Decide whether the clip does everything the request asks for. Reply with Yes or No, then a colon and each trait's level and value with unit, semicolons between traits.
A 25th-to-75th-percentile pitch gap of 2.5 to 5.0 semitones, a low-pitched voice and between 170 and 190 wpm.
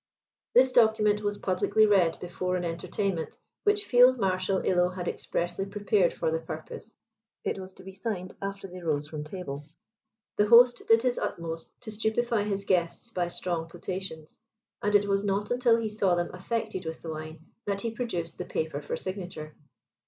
No: average, 3.9 semitones; high, 190 Hz; average, 175 wpm